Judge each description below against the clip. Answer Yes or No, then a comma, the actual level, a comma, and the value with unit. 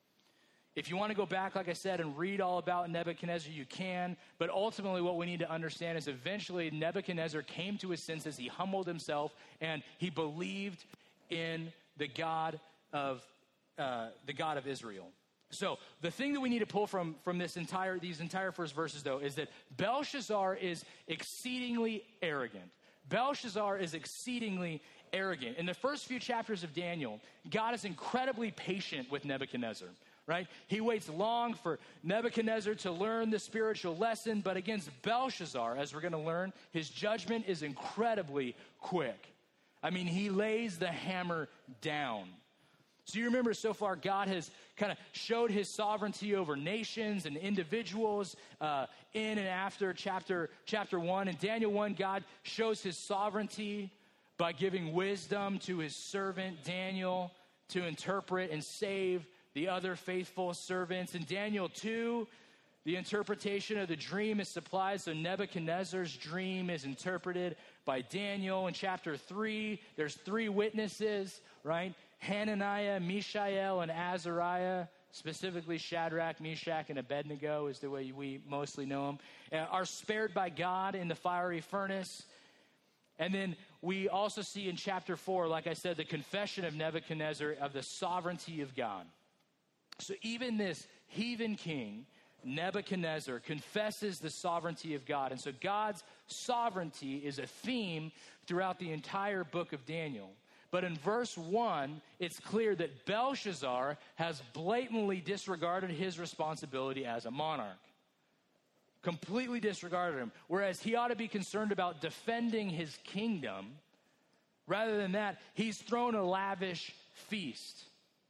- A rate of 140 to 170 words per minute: Yes, average, 145 wpm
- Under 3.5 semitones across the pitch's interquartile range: No, average, 4.1 semitones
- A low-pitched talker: No, medium, 185 Hz